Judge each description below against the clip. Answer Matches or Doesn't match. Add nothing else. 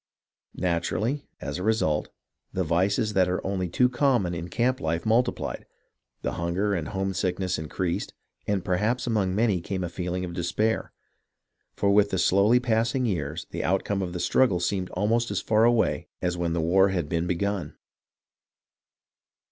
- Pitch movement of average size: Matches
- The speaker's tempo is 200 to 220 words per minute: Doesn't match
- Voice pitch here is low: Matches